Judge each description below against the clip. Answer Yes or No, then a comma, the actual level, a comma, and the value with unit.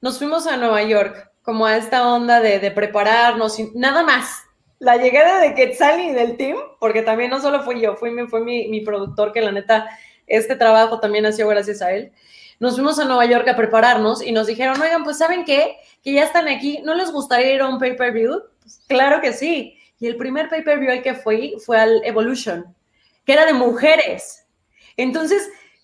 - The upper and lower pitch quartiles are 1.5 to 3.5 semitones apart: No, average, 4.4 semitones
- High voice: Yes, high, 245 Hz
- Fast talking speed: Yes, fast, 205 wpm